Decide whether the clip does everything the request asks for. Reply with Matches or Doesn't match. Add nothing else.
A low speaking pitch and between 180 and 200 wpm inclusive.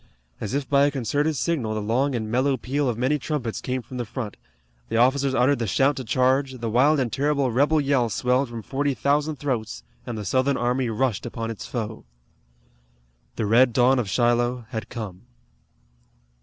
Matches